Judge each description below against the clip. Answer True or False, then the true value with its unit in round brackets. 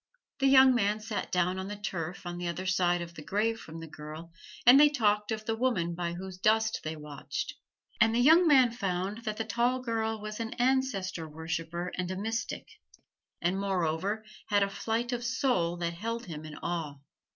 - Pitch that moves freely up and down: False (4.9 semitones)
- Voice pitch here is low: False (200 Hz)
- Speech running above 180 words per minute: True (195 wpm)